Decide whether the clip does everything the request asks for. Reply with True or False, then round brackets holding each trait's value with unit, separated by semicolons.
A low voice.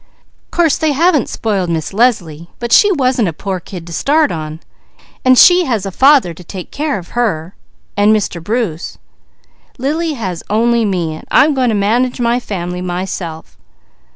False (215 Hz)